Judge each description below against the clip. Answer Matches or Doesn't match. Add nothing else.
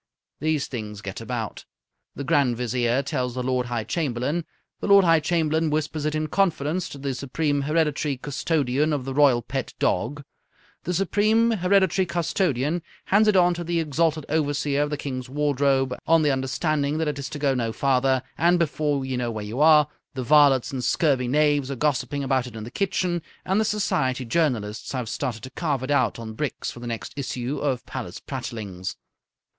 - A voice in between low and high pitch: Matches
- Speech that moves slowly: Doesn't match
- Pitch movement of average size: Matches